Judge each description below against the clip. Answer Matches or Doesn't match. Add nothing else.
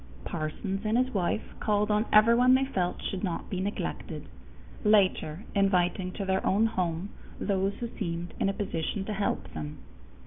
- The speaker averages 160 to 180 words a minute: Matches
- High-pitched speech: Matches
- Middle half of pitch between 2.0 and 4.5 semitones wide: Matches